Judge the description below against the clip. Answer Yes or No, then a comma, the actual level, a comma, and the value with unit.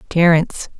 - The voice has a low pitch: No, medium, 165 Hz